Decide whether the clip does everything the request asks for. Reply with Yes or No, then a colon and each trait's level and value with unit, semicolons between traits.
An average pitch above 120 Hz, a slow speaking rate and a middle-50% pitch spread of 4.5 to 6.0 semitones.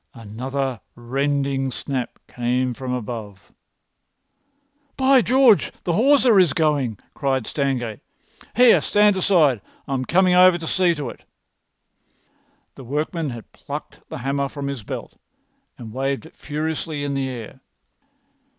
Yes: medium, 140 Hz; slow, 130 wpm; average, 5.1 semitones